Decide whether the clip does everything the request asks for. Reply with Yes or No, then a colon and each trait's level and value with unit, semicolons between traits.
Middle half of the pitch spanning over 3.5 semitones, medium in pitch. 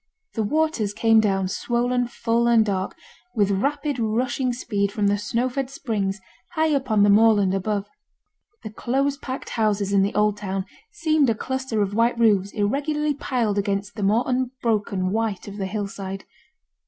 No: average, 3.9 semitones; high, 220 Hz